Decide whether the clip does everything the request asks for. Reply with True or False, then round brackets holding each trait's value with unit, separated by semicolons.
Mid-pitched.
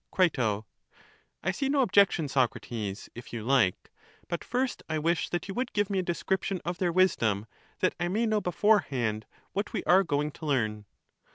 True (175 Hz)